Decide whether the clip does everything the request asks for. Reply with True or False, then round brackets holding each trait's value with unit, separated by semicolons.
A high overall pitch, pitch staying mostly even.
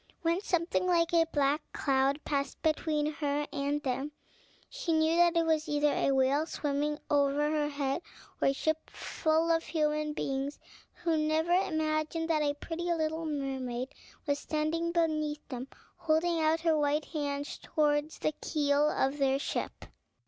True (305 Hz; 2.2 semitones)